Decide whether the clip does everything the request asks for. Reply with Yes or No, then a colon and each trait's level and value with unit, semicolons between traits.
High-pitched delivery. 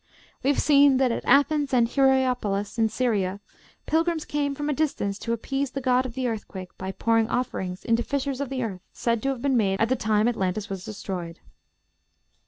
Yes: high, 245 Hz